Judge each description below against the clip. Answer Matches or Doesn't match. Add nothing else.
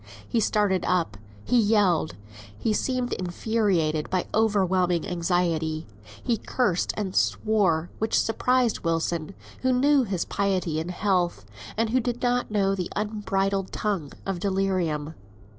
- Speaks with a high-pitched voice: Matches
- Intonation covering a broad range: Doesn't match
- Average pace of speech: Doesn't match